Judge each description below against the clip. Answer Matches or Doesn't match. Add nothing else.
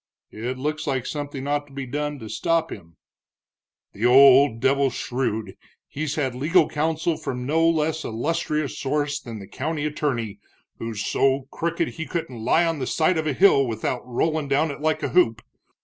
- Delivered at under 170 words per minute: Doesn't match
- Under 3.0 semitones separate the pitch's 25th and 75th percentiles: Doesn't match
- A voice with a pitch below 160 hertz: Matches